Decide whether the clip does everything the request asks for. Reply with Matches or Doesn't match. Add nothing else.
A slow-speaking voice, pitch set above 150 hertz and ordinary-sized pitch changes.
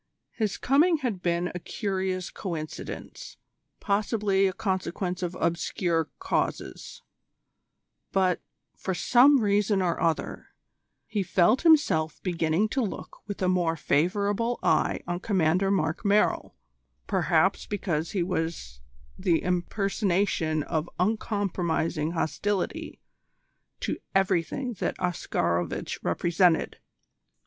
Matches